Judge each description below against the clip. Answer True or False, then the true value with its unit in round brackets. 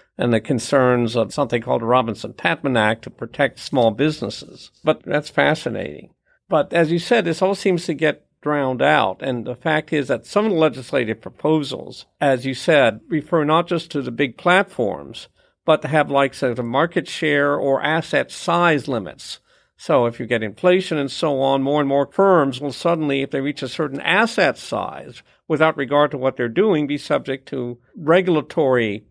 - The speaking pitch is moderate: True (145 Hz)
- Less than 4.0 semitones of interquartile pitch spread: True (3.5 semitones)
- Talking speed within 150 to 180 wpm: False (190 wpm)